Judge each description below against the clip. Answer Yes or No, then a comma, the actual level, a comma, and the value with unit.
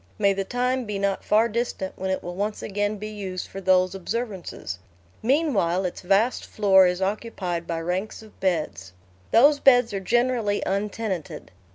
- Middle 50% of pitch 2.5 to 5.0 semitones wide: Yes, average, 3.4 semitones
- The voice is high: Yes, high, 200 Hz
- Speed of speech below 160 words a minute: No, average, 165 wpm